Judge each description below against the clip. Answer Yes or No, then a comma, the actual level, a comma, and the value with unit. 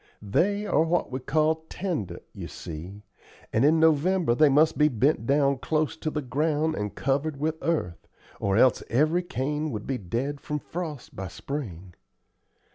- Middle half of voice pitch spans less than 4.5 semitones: No, average, 5.0 semitones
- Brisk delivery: No, average, 165 wpm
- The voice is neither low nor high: Yes, medium, 145 Hz